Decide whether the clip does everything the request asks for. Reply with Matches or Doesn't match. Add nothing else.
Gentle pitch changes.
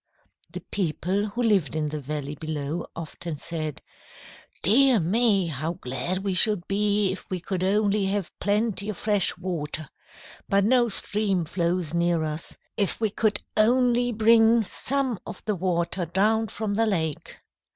Doesn't match